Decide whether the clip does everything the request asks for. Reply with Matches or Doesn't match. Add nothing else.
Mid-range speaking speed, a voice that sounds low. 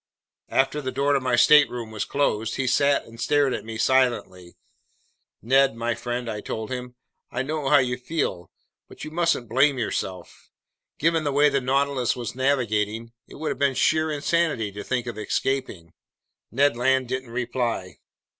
Matches